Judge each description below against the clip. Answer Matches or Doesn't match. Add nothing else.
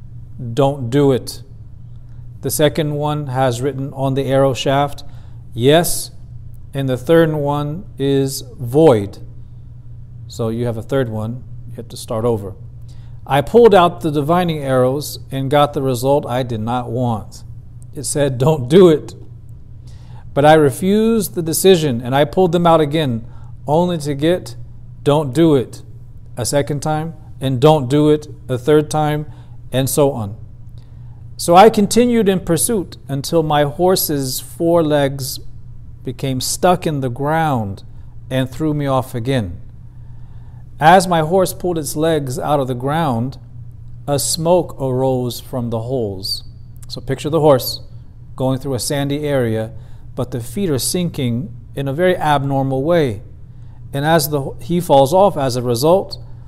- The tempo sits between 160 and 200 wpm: Doesn't match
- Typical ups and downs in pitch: Matches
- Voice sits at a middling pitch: Doesn't match